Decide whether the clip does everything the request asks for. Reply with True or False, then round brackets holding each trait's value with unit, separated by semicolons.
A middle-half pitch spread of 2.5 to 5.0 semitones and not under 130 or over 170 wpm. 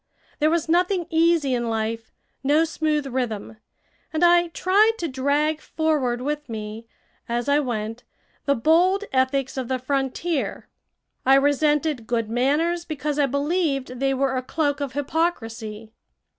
True (4.2 semitones; 145 wpm)